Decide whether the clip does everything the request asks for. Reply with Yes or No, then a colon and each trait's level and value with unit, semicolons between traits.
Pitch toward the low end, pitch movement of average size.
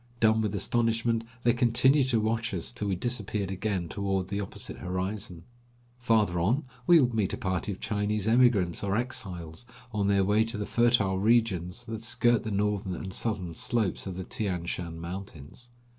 Yes: low, 105 Hz; average, 3.5 semitones